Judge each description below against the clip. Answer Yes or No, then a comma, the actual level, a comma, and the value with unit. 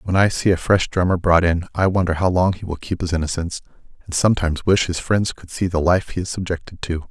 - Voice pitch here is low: Yes, very low, 90 Hz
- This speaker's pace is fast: Yes, fast, 255 wpm